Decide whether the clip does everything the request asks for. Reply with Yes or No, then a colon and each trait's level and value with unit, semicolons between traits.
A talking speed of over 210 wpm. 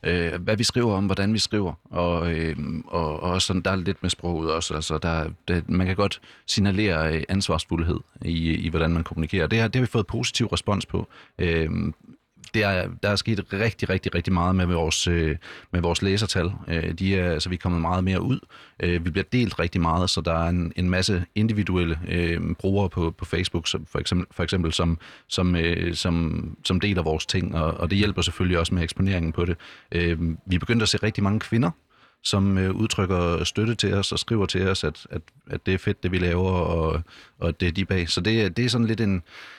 Yes: fast, 225 wpm